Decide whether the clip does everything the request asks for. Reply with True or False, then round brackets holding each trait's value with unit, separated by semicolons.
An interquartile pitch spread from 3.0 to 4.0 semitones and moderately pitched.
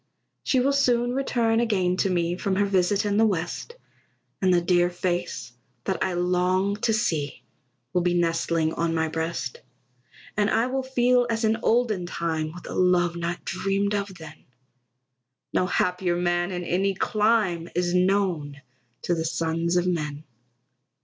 True (3.3 semitones; 180 Hz)